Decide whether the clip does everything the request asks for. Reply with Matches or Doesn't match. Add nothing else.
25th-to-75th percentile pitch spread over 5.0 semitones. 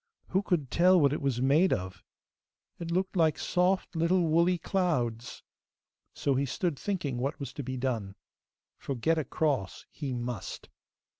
Matches